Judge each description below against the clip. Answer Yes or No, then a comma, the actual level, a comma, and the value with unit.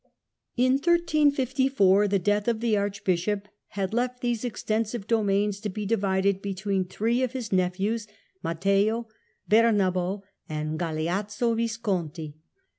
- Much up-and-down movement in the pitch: No, average, 3.4 semitones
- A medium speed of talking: No, slow, 115 wpm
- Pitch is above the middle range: Yes, high, 205 Hz